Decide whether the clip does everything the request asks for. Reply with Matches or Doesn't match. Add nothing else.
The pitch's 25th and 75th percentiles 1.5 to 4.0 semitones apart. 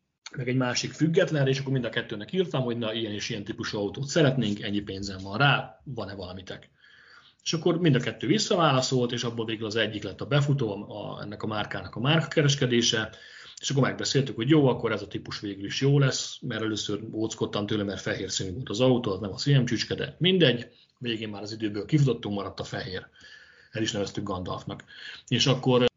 Doesn't match